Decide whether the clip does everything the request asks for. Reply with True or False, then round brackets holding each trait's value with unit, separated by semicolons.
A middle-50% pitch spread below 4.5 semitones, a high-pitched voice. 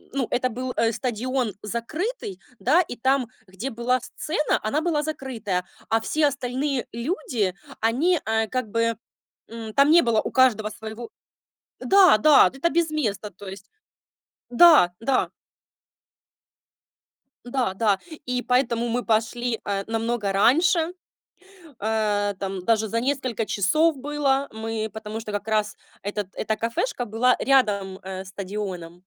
True (4.1 semitones; 230 Hz)